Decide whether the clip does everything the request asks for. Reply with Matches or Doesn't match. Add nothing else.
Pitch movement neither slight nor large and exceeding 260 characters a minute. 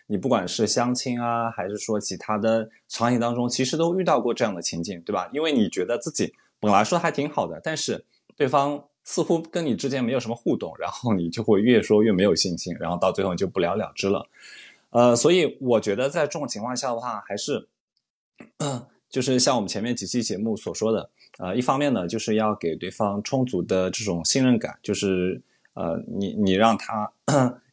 Matches